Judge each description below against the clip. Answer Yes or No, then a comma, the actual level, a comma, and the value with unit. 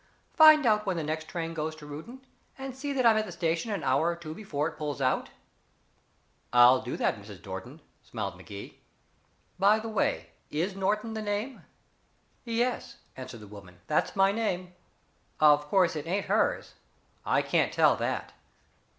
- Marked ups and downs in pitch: Yes, wide, 6.7 semitones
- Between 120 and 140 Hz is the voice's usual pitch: No, medium, 170 Hz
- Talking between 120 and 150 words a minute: No, average, 170 wpm